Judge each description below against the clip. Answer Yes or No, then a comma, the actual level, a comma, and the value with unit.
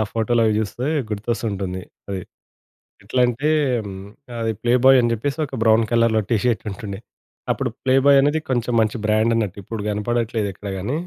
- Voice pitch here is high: No, low, 115 Hz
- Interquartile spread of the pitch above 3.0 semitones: No, narrow, 2.5 semitones